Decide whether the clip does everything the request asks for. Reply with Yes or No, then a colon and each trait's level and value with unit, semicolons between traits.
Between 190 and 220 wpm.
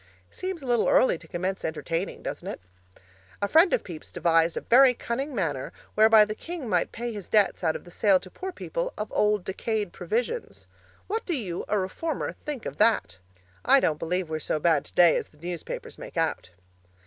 Yes: average, 195 wpm